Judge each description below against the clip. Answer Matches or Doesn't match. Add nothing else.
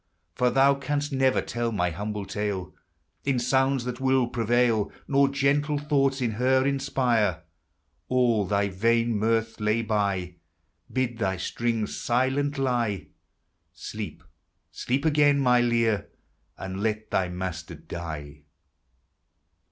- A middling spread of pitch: Matches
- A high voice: Doesn't match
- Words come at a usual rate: Doesn't match